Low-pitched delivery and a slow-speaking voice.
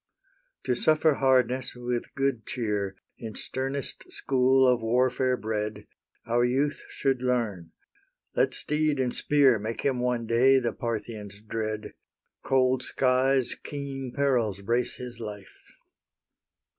Yes: low, 125 Hz; slow, 120 wpm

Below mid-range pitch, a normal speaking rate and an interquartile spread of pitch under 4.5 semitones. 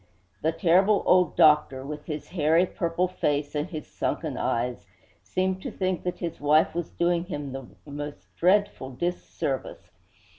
No: medium, 160 Hz; average, 155 wpm; average, 3.6 semitones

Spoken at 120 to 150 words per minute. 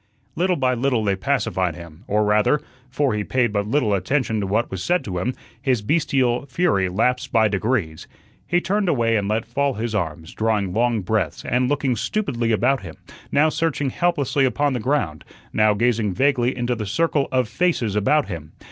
No: average, 185 wpm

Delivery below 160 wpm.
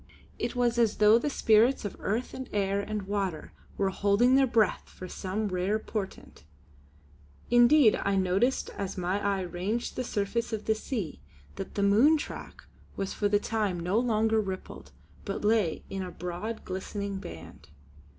No: average, 165 wpm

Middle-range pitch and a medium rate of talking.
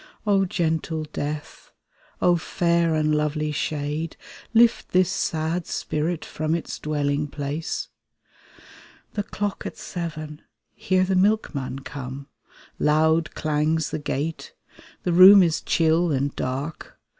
No: medium, 160 Hz; slow, 120 wpm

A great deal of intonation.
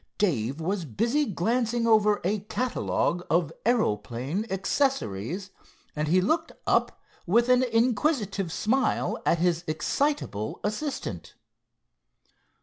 Yes: wide, 6.4 semitones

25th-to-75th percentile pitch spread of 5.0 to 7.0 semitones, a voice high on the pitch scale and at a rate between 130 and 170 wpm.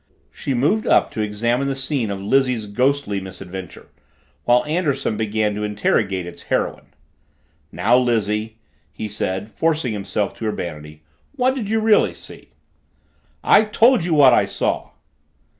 No: wide, 5.6 semitones; low, 115 Hz; average, 140 wpm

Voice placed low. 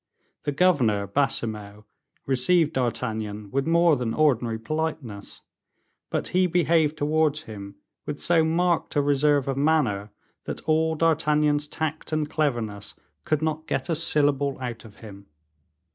No: medium, 145 Hz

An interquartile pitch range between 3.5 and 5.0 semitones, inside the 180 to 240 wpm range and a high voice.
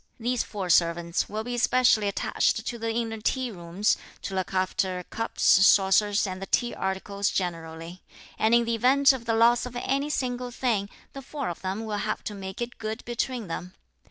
Yes: average, 4.1 semitones; average, 190 wpm; high, 215 Hz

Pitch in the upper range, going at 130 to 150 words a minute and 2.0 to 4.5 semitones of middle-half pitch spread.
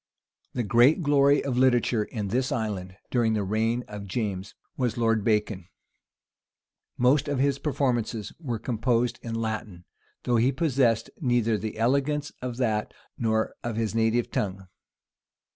No: low, 115 Hz; average, 145 wpm; average, 3.0 semitones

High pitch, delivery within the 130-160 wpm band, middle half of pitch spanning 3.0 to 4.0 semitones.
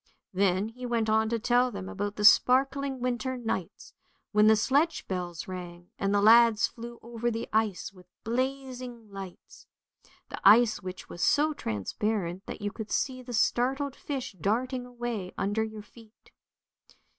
Yes: high, 220 Hz; average, 155 wpm; average, 3.7 semitones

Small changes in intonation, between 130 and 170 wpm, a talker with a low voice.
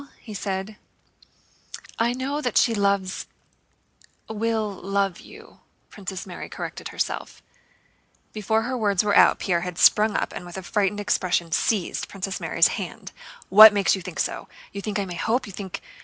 No: narrow, 2.3 semitones; average, 165 wpm; high, 200 Hz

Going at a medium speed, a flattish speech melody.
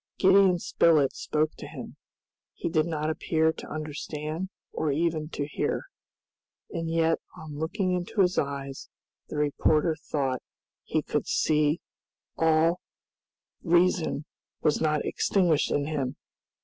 No: slow, 130 wpm; narrow, 2.1 semitones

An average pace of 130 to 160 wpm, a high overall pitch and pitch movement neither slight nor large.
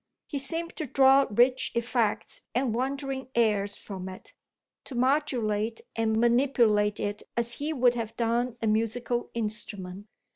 Yes: average, 140 wpm; high, 235 Hz; average, 3.6 semitones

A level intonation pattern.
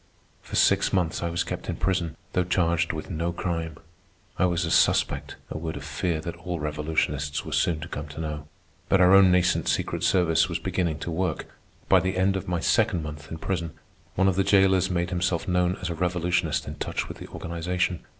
Yes: narrow, 2.0 semitones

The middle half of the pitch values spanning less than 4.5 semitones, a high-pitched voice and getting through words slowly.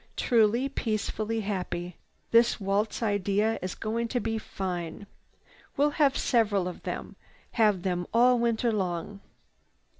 Yes: average, 3.3 semitones; high, 215 Hz; slow, 130 wpm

